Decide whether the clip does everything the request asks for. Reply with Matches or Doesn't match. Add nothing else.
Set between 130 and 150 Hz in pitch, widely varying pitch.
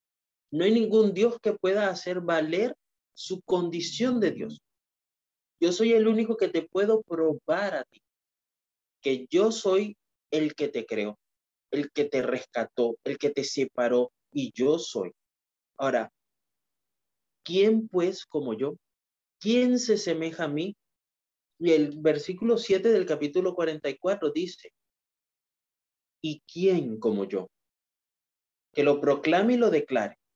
Doesn't match